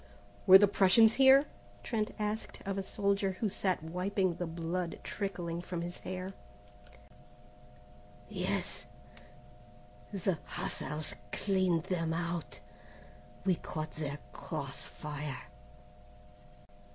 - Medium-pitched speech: Yes, medium, 180 Hz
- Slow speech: Yes, slow, 105 wpm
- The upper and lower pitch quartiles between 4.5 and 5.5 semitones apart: No, average, 3.2 semitones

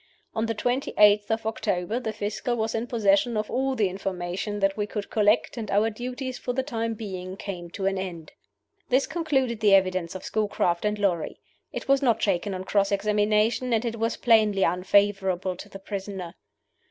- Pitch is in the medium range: No, high, 210 Hz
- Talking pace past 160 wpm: Yes, average, 190 wpm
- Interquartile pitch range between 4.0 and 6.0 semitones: No, average, 2.9 semitones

